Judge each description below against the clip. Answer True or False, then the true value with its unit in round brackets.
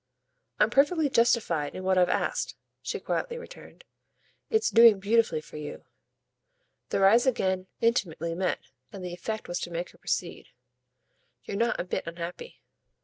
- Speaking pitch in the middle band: False (195 Hz)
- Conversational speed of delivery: True (150 wpm)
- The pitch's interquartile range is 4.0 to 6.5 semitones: True (5.1 semitones)